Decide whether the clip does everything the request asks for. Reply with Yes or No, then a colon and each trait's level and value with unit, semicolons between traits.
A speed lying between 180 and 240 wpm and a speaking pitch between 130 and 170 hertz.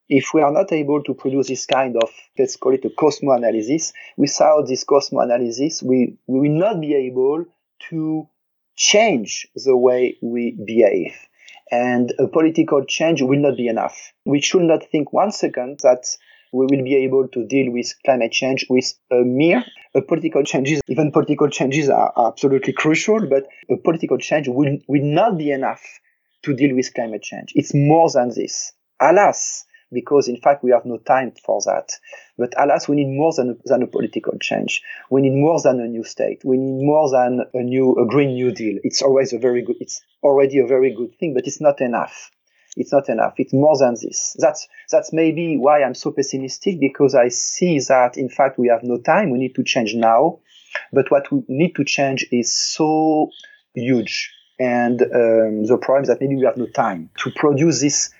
Yes: average, 195 wpm; low, 135 Hz